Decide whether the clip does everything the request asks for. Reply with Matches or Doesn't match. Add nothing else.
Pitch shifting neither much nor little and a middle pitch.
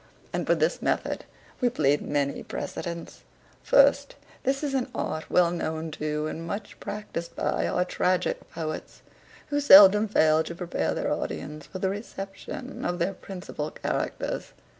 Matches